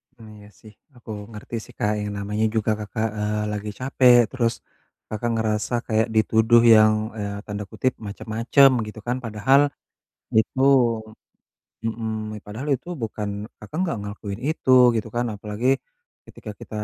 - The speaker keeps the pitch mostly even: Yes, narrow, 2.0 semitones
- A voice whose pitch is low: Yes, low, 110 Hz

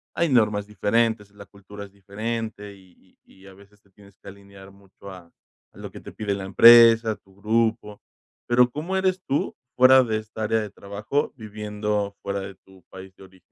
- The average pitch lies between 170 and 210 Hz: No, low, 105 Hz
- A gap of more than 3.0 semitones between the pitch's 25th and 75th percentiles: No, narrow, 2.4 semitones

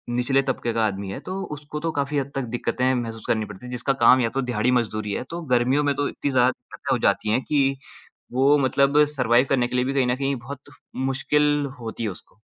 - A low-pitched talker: Yes, low, 130 Hz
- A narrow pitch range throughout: No, average, 3.0 semitones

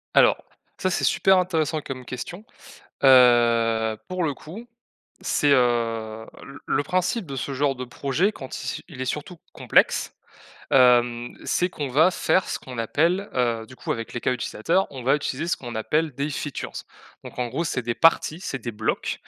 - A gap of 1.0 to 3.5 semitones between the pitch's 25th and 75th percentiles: No, average, 5.2 semitones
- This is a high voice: No, low, 135 Hz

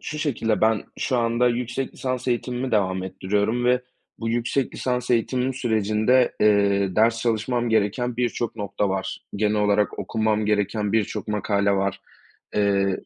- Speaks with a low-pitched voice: Yes, low, 110 Hz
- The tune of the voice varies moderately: Yes, average, 3.2 semitones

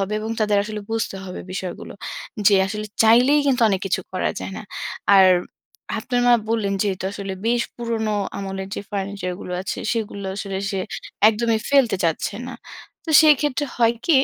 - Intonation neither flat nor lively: Yes, average, 3.3 semitones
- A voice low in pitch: No, high, 210 Hz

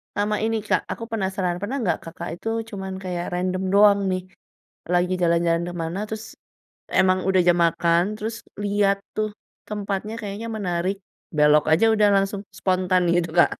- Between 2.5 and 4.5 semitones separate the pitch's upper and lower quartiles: Yes, average, 2.8 semitones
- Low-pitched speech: No, high, 190 Hz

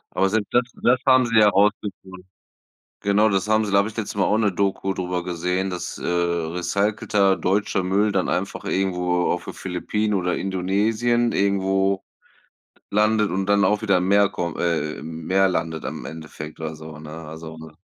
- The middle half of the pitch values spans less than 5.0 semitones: Yes, average, 2.8 semitones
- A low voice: Yes, very low, 95 Hz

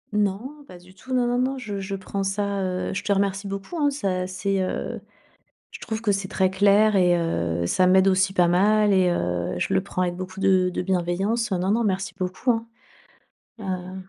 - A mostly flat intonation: Yes, narrow, 2.1 semitones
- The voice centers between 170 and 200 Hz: Yes, high, 190 Hz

